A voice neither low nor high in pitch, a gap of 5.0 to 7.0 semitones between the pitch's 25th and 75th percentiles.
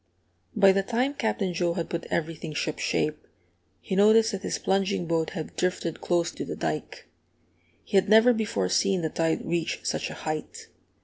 No: medium, 180 Hz; average, 3.5 semitones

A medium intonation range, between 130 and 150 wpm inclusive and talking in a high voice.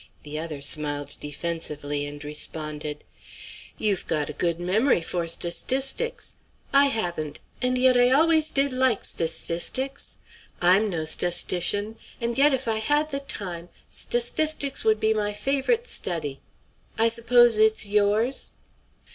No: wide, 7.8 semitones; average, 145 wpm; high, 210 Hz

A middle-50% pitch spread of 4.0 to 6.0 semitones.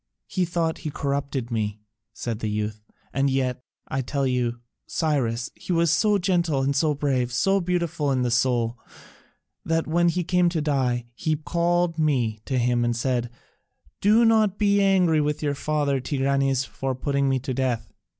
Yes: average, 5.1 semitones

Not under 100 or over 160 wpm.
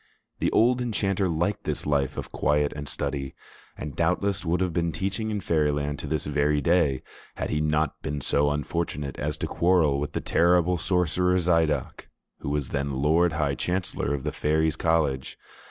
No: average, 175 wpm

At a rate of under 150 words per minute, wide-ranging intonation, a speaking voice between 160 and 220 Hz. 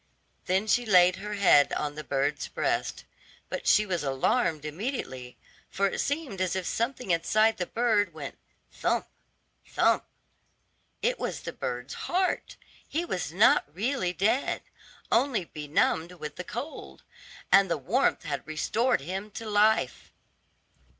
Yes: average, 140 wpm; wide, 6.4 semitones; high, 190 Hz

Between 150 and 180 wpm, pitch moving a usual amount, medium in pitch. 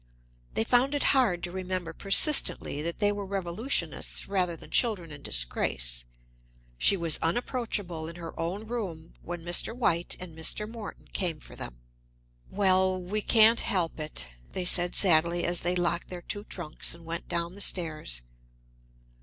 Yes: average, 160 wpm; average, 3.5 semitones; medium, 175 Hz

